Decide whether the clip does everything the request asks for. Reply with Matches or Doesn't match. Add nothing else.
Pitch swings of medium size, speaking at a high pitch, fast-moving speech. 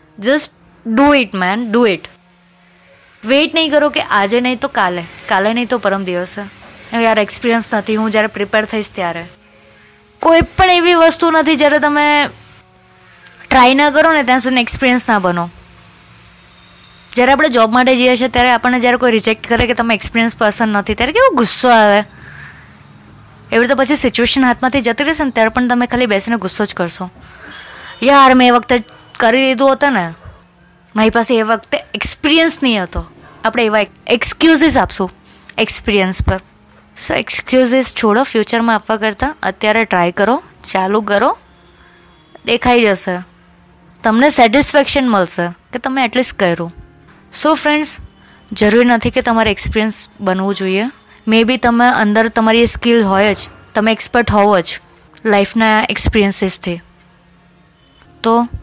Matches